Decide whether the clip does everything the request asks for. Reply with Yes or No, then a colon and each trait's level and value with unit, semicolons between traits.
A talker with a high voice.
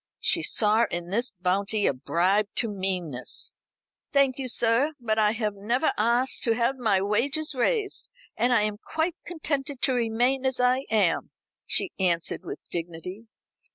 Yes: high, 225 Hz